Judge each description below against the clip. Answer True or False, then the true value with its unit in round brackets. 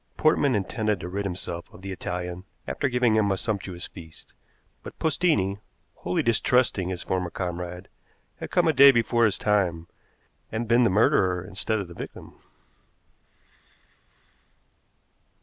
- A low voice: True (95 Hz)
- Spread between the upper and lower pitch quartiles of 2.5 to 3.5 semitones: False (4.3 semitones)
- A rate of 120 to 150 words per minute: True (140 wpm)